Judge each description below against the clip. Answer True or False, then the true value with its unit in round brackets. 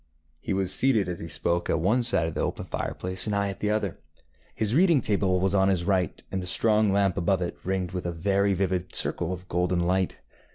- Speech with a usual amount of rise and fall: False (2.1 semitones)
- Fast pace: True (240 wpm)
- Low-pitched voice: True (95 Hz)